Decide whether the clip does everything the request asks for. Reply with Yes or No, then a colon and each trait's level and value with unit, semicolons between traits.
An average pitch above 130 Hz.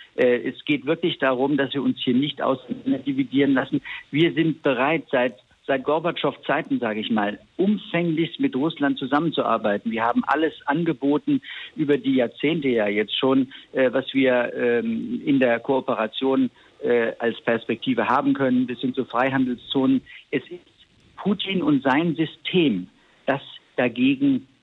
Yes: medium, 140 Hz